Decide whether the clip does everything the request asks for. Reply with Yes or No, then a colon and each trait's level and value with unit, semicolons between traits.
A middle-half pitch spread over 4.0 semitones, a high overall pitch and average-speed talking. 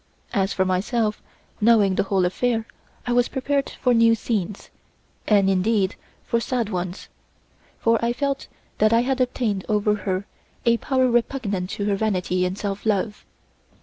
No: average, 3.6 semitones; high, 215 Hz; average, 155 wpm